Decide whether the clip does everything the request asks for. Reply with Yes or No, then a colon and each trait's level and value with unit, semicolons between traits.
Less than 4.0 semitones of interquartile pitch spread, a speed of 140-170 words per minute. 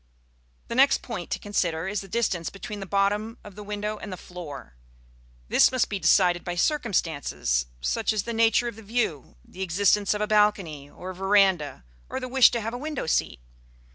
No: average, 3.6 semitones; average, 195 wpm